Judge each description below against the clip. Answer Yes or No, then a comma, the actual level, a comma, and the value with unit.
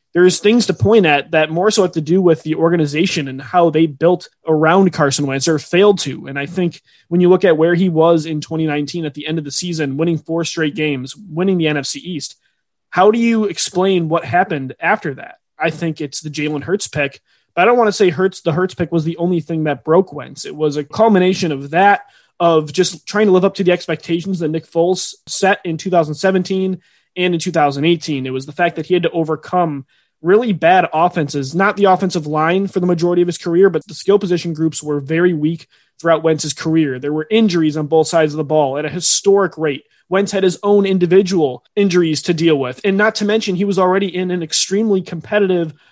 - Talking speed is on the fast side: Yes, fast, 225 wpm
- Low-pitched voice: No, medium, 170 Hz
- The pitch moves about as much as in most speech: Yes, average, 3.2 semitones